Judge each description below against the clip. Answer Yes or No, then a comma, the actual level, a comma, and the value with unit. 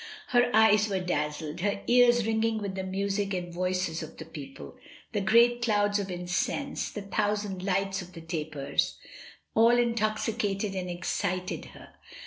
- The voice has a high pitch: Yes, high, 195 Hz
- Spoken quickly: No, average, 155 wpm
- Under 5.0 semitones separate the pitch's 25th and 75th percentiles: Yes, average, 3.3 semitones